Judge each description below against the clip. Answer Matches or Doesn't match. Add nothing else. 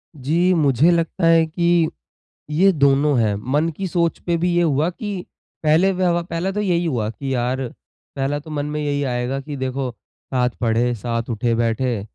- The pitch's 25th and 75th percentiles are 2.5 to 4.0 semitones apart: Doesn't match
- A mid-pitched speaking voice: Matches